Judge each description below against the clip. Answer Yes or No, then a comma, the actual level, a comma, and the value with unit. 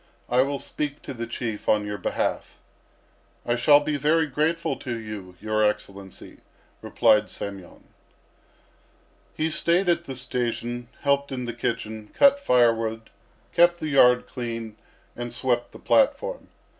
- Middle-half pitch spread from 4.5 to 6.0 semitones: Yes, average, 4.9 semitones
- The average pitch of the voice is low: Yes, low, 125 Hz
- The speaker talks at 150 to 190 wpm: No, average, 140 wpm